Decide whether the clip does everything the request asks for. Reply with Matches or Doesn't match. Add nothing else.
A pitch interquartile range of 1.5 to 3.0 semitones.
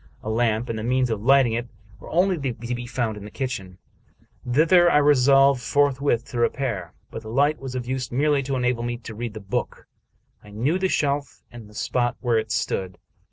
Doesn't match